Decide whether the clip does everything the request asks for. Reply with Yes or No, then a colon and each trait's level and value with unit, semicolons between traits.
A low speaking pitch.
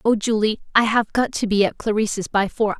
No: high, 215 Hz